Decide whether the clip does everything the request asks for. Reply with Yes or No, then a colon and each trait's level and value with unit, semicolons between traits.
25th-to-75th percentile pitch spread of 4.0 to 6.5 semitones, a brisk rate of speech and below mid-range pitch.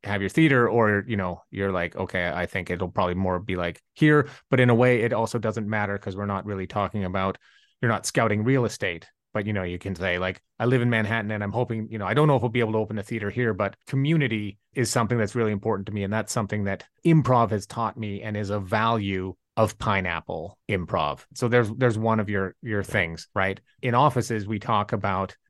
No: average, 3.2 semitones; fast, 240 wpm; low, 105 Hz